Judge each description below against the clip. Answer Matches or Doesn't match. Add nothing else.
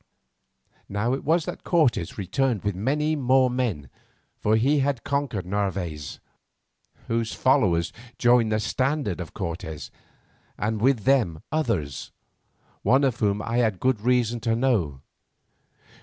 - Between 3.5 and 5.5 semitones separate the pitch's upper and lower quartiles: Matches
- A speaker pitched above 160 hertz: Doesn't match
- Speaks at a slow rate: Matches